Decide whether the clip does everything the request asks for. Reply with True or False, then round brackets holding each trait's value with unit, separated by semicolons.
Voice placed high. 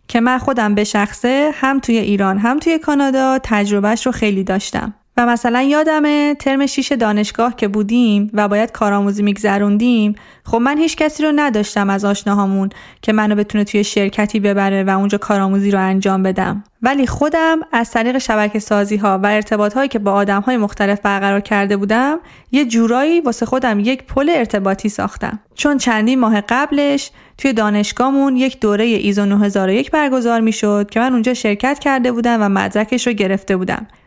True (220 Hz)